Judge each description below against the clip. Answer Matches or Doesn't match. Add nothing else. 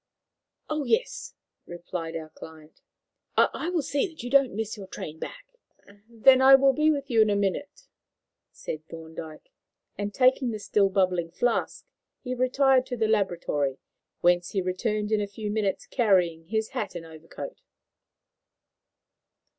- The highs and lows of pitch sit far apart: Matches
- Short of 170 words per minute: Matches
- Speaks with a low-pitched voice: Doesn't match